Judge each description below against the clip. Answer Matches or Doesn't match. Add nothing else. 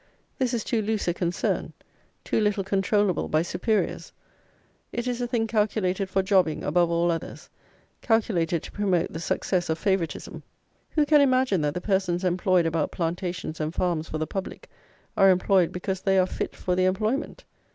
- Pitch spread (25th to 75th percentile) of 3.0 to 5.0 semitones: Matches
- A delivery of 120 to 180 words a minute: Matches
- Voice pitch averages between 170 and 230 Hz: Matches